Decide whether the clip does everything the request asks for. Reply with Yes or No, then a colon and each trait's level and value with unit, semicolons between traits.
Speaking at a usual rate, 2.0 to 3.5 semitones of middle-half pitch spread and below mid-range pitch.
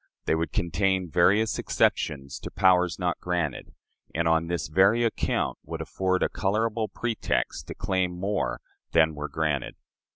Yes: average, 150 wpm; average, 3.2 semitones; very low, 90 Hz